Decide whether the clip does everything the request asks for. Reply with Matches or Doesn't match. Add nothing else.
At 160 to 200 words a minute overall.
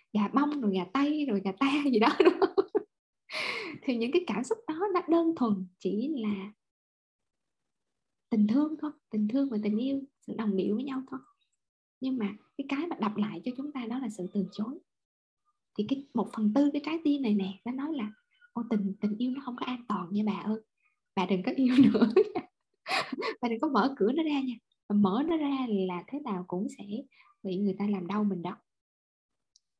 Doesn't match